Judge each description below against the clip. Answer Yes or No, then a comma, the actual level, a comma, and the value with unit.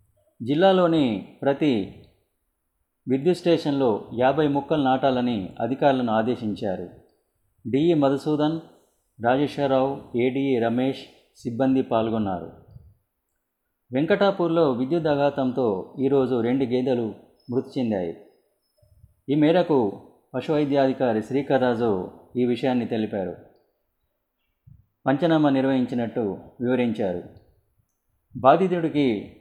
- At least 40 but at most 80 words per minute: Yes, slow, 70 wpm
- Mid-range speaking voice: No, low, 130 Hz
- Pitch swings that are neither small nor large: Yes, average, 3.7 semitones